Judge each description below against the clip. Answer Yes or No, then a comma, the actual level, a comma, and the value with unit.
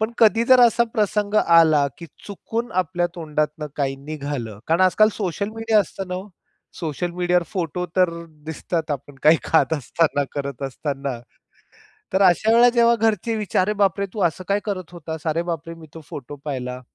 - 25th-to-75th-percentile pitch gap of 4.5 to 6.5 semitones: Yes, average, 5.2 semitones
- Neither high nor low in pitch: Yes, medium, 175 Hz